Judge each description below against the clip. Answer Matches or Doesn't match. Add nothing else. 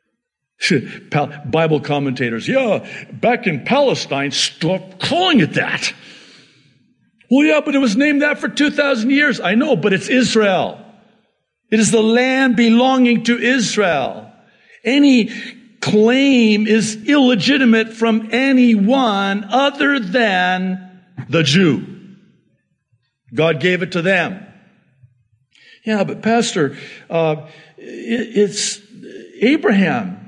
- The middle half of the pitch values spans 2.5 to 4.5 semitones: Doesn't match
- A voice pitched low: Doesn't match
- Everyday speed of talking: Doesn't match